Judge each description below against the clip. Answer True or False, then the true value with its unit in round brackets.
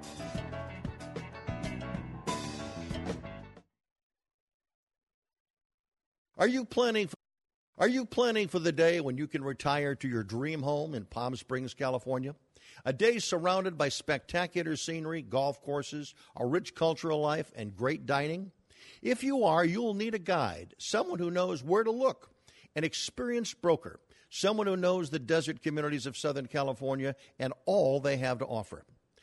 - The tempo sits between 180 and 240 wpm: False (140 wpm)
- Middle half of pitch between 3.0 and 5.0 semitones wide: False (5.5 semitones)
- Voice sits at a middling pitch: True (150 Hz)